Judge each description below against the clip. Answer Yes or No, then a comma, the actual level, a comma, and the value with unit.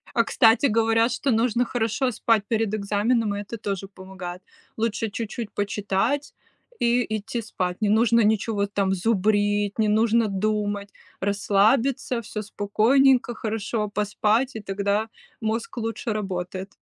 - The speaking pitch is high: Yes, high, 215 Hz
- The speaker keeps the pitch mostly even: Yes, narrow, 2.1 semitones